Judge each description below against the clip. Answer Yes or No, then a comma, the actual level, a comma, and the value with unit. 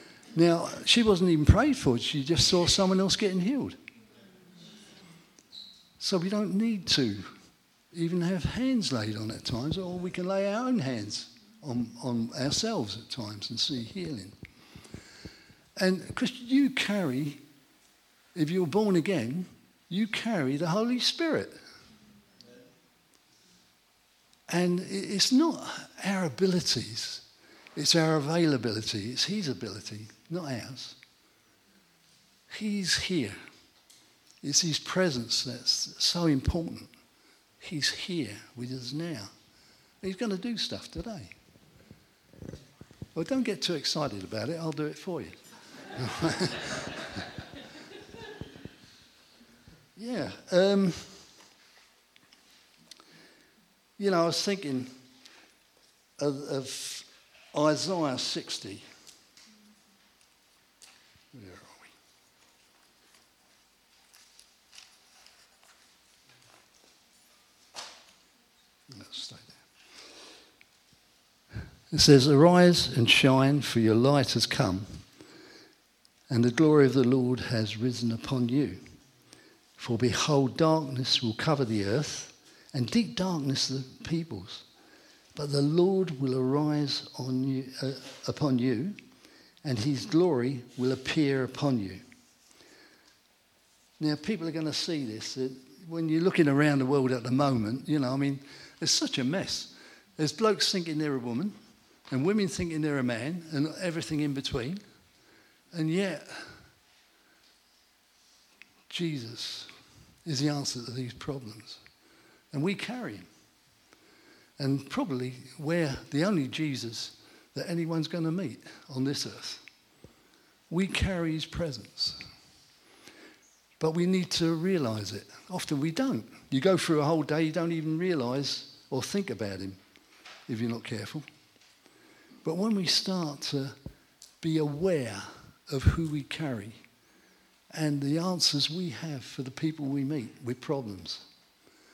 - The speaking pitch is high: No, medium, 150 Hz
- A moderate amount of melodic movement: No, wide, 5.8 semitones